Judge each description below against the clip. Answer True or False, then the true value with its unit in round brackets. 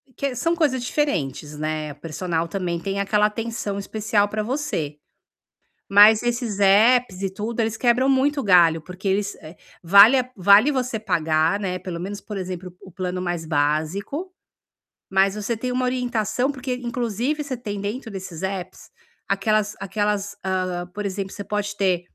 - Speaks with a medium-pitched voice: False (200 Hz)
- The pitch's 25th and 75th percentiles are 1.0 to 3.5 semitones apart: False (4.6 semitones)